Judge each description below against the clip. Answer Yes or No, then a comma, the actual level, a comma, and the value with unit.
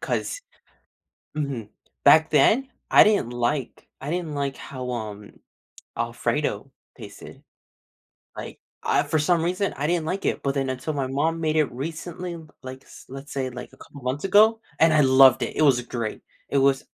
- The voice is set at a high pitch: No, medium, 140 Hz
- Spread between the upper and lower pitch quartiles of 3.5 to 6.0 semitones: Yes, average, 4.0 semitones